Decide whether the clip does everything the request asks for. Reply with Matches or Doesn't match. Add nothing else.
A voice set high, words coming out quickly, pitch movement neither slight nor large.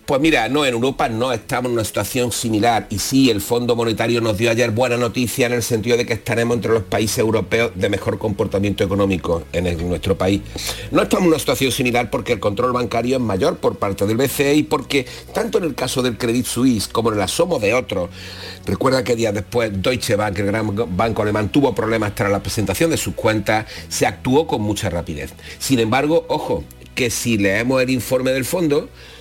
Doesn't match